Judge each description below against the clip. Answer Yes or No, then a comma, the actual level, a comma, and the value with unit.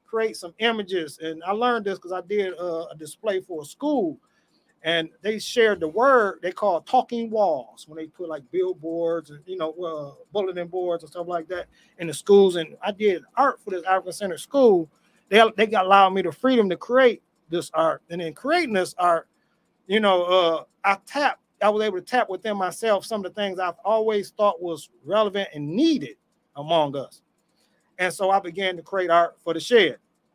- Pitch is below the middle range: No, medium, 185 Hz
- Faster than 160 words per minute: Yes, fast, 205 wpm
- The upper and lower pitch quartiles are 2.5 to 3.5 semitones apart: No, average, 3.9 semitones